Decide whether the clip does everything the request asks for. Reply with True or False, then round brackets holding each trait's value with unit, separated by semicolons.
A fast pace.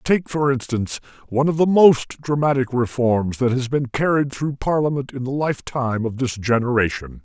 False (175 wpm)